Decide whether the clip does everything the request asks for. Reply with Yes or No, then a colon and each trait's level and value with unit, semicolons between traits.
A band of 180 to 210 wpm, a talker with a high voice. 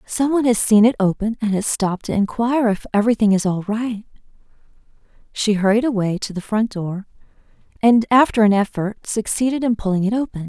Yes: average, 185 wpm; high, 215 Hz